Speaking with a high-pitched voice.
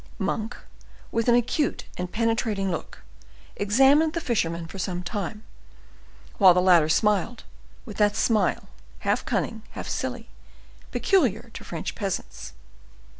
Yes: high, 210 Hz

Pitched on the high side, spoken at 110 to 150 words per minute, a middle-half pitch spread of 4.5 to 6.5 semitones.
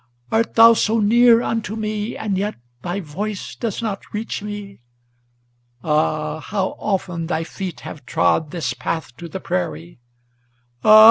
Yes: high, 195 Hz; average, 145 wpm; average, 5.3 semitones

